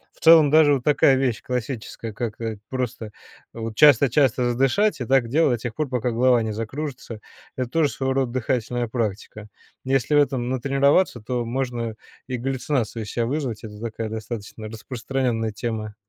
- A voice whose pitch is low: Yes, low, 125 Hz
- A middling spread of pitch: Yes, average, 3.1 semitones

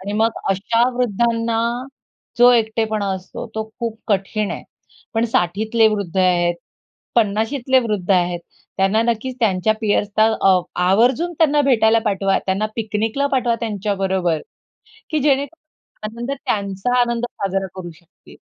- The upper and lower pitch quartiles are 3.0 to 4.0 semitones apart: Yes, average, 3.4 semitones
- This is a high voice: Yes, high, 220 Hz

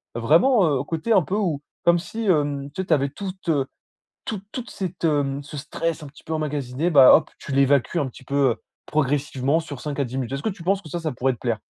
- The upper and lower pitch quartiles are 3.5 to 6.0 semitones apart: Yes, average, 3.9 semitones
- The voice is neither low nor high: Yes, medium, 150 Hz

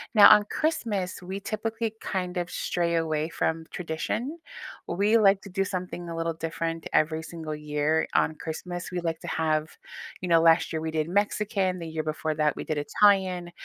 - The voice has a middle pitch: Yes, medium, 170 Hz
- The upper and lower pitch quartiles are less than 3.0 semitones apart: No, average, 3.4 semitones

